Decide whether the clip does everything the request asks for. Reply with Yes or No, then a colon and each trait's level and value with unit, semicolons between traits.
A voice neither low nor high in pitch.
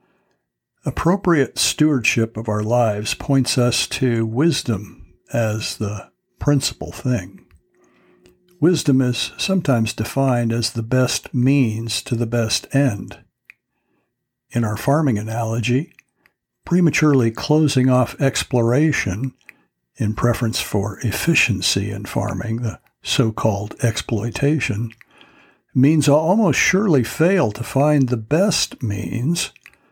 No: low, 120 Hz